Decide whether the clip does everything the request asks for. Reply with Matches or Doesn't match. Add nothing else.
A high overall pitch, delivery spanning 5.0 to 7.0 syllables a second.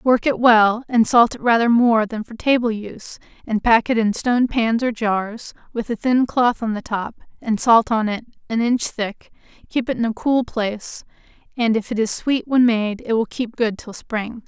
Doesn't match